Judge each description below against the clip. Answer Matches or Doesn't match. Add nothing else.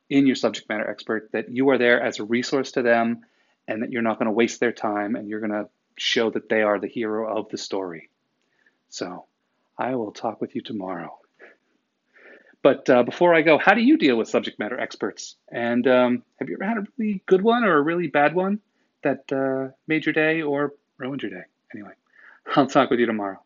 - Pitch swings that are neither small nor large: Doesn't match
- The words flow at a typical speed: Doesn't match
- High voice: Doesn't match